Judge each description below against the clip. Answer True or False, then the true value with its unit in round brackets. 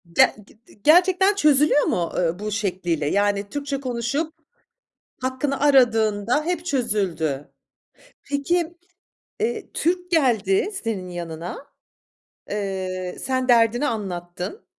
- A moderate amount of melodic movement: False (7.5 semitones)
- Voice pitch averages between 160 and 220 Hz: False (230 Hz)